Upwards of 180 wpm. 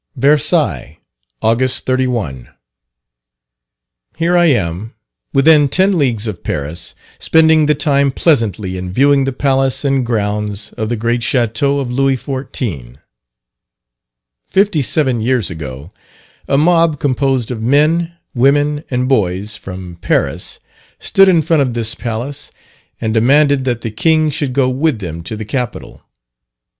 No: slow, 135 wpm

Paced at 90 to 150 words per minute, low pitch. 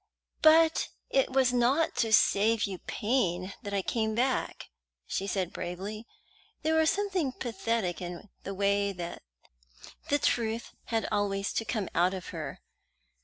No: average, 140 wpm; high, 215 Hz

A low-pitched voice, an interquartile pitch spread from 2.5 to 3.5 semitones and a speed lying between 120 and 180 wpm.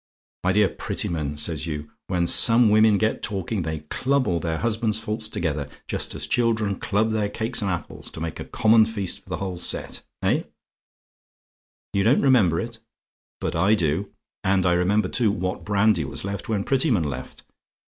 No: low, 100 Hz; average, 4.3 semitones; average, 175 wpm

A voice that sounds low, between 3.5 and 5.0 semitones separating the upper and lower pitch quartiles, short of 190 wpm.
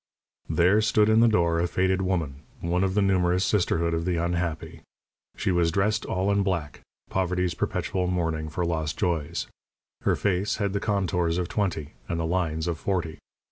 No: very low, 90 Hz; narrow, 2.6 semitones; average, 180 wpm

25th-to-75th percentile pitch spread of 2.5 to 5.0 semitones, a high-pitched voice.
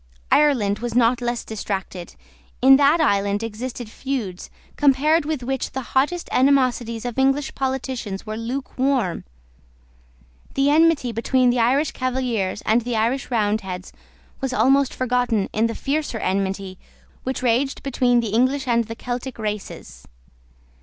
Yes: average, 3.4 semitones; high, 245 Hz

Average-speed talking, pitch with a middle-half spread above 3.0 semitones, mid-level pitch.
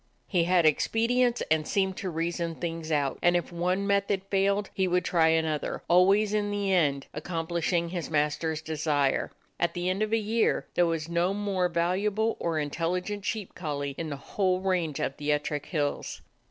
Yes: average, 180 wpm; average, 3.6 semitones; medium, 175 Hz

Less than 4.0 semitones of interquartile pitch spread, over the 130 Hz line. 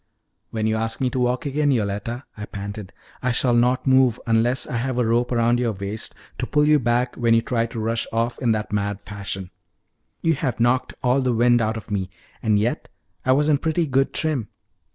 No: average, 2.7 semitones; low, 120 Hz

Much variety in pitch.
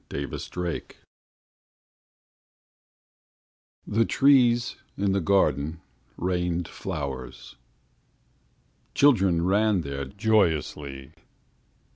Yes: wide, 6.4 semitones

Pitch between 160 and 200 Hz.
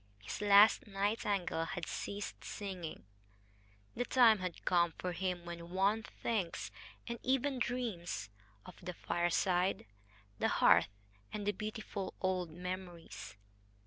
Yes: high, 190 Hz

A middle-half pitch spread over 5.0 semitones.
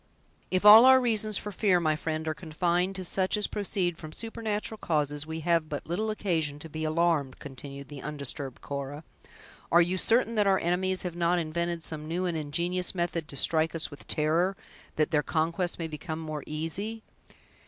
No: average, 3.3 semitones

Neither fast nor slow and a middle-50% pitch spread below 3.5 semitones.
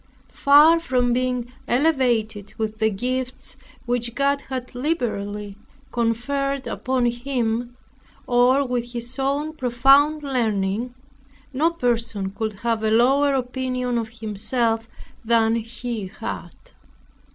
No: slow, 110 wpm; average, 2.7 semitones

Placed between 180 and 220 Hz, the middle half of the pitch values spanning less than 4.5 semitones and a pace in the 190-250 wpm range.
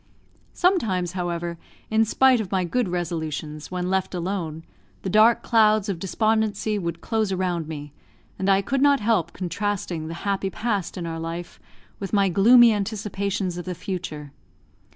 No: high, 190 Hz; average, 3.9 semitones; average, 155 wpm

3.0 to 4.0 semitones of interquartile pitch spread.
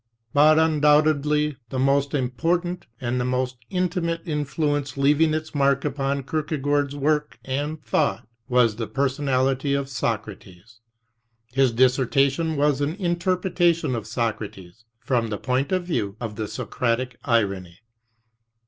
Yes: average, 3.6 semitones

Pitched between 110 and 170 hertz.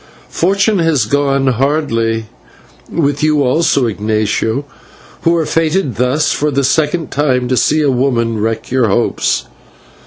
Yes: medium, 140 Hz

